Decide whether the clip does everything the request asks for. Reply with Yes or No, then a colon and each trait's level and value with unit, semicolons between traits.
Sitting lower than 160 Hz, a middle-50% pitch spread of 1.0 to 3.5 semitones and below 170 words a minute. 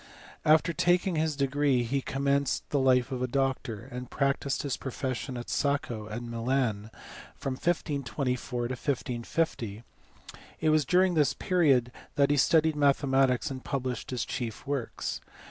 Yes: low, 135 Hz; average, 2.8 semitones; average, 140 wpm